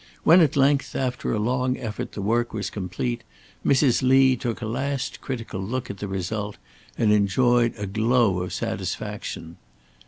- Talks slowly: No, average, 160 wpm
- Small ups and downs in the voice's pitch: No, average, 3.8 semitones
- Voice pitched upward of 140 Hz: No, low, 120 Hz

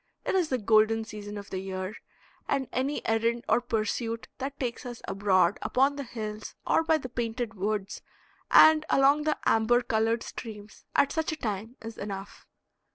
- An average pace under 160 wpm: No, average, 170 wpm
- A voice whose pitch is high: Yes, high, 225 Hz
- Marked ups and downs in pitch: No, average, 3.7 semitones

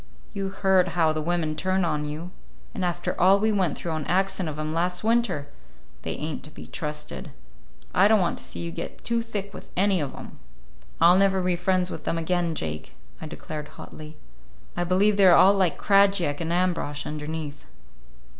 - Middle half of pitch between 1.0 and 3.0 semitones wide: No, average, 3.8 semitones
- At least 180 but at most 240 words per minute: Yes, average, 190 wpm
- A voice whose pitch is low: No, medium, 175 Hz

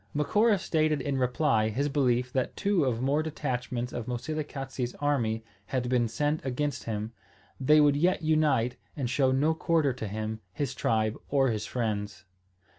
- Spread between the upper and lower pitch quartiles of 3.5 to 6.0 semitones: Yes, average, 3.9 semitones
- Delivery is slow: No, average, 160 wpm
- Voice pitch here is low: Yes, low, 130 Hz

